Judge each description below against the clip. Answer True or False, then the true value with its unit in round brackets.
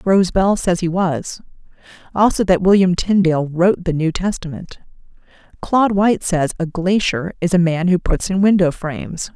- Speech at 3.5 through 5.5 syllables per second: True (5.0 syllables/s)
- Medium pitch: True (180 Hz)